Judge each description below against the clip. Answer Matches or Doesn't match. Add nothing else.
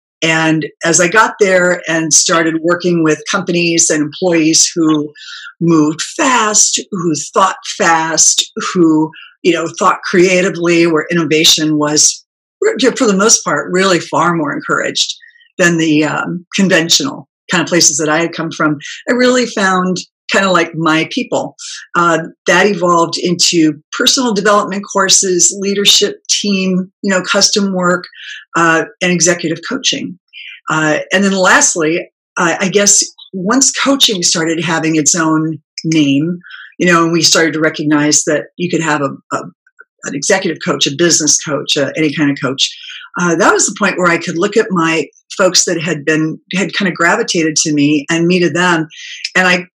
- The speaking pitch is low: Doesn't match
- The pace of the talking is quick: Doesn't match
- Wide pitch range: Doesn't match